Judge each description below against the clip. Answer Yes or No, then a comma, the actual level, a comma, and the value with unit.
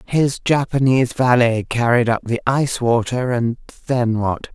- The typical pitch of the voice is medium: No, low, 120 Hz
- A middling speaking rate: No, slow, 130 wpm